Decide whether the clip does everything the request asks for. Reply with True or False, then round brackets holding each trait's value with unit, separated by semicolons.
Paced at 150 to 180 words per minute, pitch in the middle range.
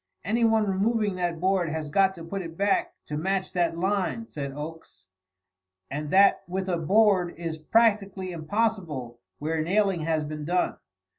True (155 wpm; 180 Hz)